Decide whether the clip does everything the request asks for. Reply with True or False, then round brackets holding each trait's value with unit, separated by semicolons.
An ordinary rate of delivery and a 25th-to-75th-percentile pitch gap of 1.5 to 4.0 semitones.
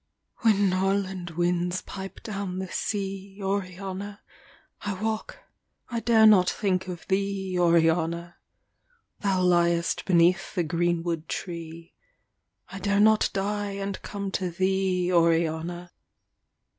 False (115 wpm; 2.4 semitones)